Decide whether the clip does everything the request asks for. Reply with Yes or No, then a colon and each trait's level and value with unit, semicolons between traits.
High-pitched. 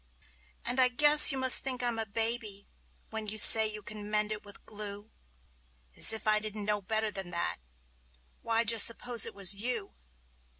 Yes: high, 215 Hz